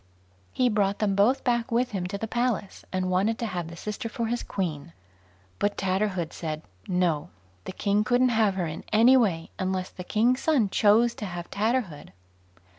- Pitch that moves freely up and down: No, average, 4.1 semitones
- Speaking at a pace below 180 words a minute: No, average, 185 wpm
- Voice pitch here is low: No, high, 205 Hz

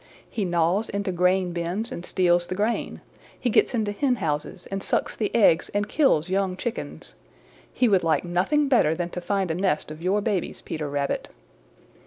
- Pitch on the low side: No, medium, 185 Hz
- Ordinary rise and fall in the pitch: Yes, average, 3.3 semitones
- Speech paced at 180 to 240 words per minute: Yes, average, 185 wpm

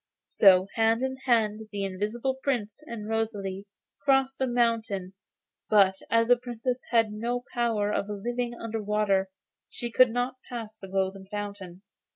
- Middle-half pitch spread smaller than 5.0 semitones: Yes, average, 3.1 semitones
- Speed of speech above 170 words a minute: No, average, 150 wpm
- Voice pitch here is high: Yes, high, 220 Hz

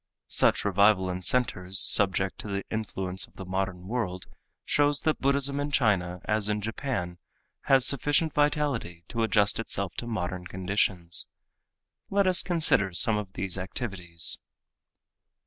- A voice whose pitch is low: Yes, low, 100 Hz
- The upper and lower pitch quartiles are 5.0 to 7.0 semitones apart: Yes, wide, 5.5 semitones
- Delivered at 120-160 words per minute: Yes, average, 140 wpm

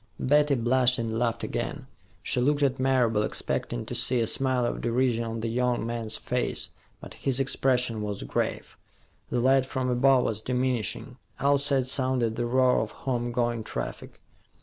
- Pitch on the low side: Yes, low, 125 Hz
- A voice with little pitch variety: Yes, narrow, 2.1 semitones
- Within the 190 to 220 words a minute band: No, average, 165 wpm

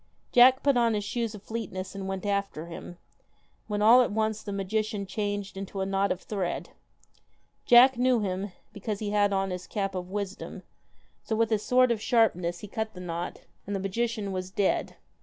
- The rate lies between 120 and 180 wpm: No, average, 195 wpm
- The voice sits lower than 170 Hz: No, high, 205 Hz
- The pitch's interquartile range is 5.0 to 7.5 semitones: No, narrow, 2.5 semitones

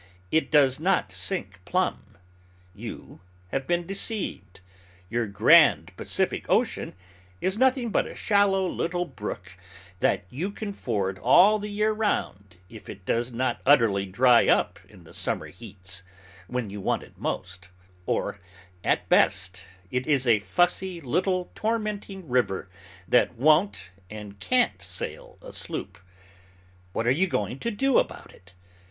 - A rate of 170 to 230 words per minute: No, average, 145 wpm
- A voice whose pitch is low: Yes, low, 125 Hz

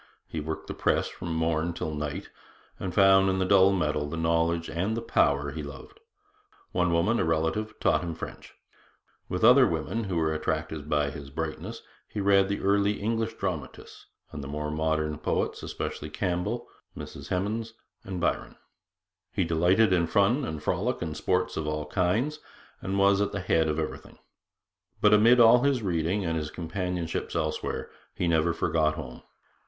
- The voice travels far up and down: No, average, 4.2 semitones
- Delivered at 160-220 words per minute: Yes, average, 170 wpm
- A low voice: Yes, very low, 85 Hz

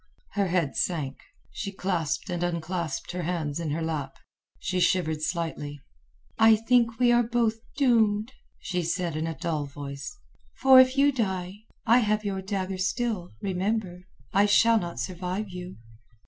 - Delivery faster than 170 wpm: No, average, 155 wpm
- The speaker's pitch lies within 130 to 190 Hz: Yes, medium, 185 Hz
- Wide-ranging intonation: No, average, 4.6 semitones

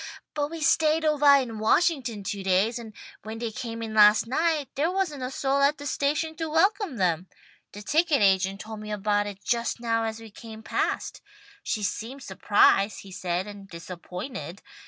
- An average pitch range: No, wide, 5.9 semitones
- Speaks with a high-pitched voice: Yes, high, 225 Hz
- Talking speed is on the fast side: No, average, 180 wpm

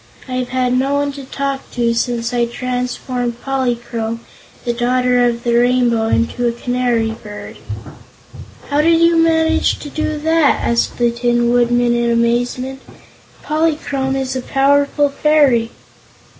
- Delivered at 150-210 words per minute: No, average, 140 wpm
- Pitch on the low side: No, very high, 250 Hz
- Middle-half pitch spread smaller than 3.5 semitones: Yes, average, 2.7 semitones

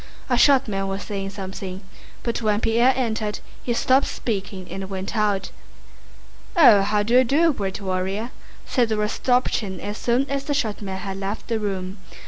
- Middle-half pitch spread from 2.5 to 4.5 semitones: Yes, average, 3.6 semitones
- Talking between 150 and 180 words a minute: Yes, average, 170 wpm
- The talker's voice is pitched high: Yes, high, 210 Hz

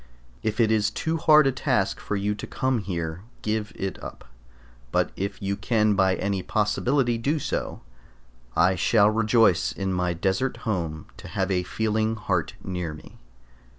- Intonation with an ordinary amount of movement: Yes, average, 3.3 semitones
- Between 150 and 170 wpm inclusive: Yes, average, 165 wpm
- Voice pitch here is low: Yes, low, 105 Hz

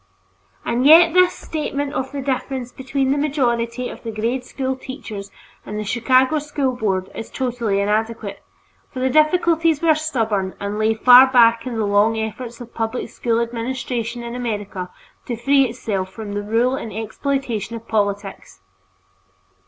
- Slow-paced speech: No, average, 160 wpm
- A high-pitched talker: Yes, high, 235 Hz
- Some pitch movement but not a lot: Yes, average, 3.4 semitones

